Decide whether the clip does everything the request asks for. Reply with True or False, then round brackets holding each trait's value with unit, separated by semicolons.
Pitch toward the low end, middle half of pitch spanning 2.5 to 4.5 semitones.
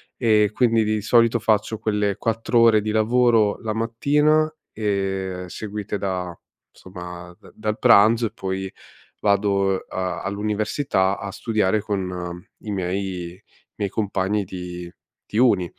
True (105 Hz; 2.8 semitones)